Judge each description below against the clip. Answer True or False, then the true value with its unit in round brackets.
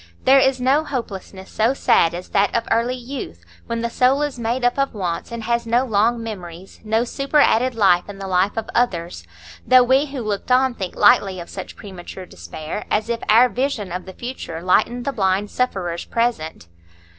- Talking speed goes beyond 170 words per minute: True (190 wpm)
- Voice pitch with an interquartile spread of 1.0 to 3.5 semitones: False (4.9 semitones)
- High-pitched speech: True (225 Hz)